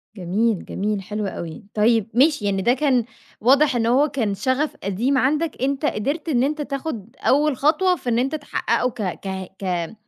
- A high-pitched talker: Yes, high, 245 Hz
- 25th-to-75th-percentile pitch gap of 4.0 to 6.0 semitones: Yes, wide, 5.5 semitones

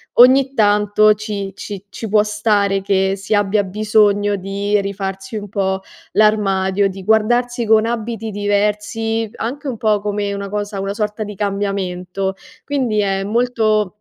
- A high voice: Yes, high, 205 Hz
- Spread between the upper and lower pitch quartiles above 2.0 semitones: No, narrow, 1.7 semitones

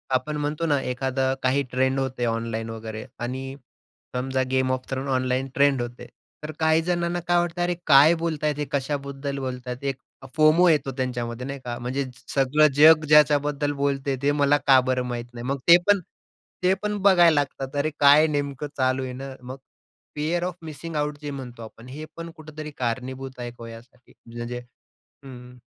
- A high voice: No, low, 135 Hz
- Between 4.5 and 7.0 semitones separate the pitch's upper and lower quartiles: No, average, 3.0 semitones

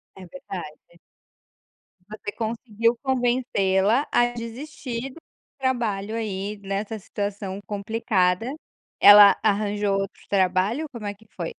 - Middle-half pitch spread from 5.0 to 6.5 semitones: No, average, 3.3 semitones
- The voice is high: Yes, high, 210 Hz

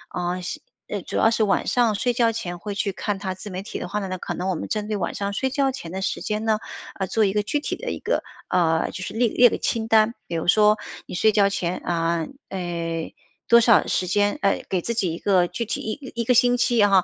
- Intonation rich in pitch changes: No, average, 3.6 semitones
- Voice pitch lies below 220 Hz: Yes, high, 205 Hz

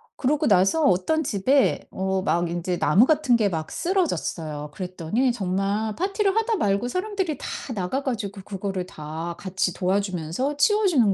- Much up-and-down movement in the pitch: Yes, wide, 8.2 semitones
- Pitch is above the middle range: Yes, high, 200 Hz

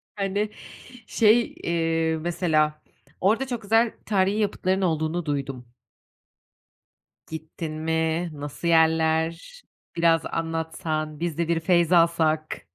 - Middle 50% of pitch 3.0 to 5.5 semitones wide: No, narrow, 2.5 semitones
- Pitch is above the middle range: No, medium, 165 Hz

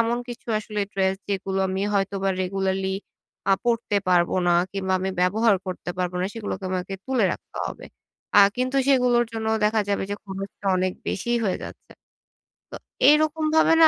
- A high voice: Yes, high, 200 Hz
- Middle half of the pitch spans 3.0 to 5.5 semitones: Yes, average, 3.8 semitones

